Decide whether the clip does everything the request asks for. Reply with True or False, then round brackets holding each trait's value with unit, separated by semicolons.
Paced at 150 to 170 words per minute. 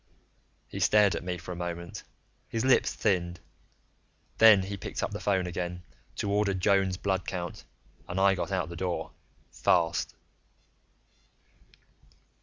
False (140 wpm)